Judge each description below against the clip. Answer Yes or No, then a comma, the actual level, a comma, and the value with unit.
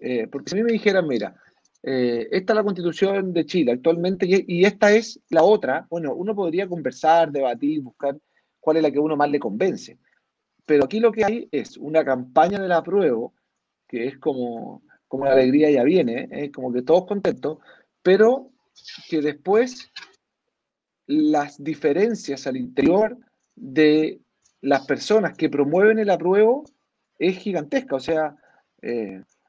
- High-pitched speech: No, medium, 165 Hz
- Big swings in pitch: Yes, wide, 6.2 semitones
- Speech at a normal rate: Yes, average, 165 wpm